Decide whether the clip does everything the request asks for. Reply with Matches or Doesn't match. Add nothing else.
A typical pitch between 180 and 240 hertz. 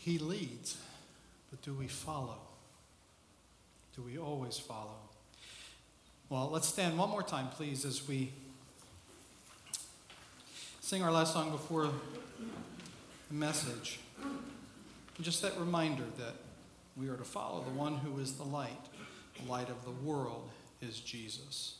Doesn't match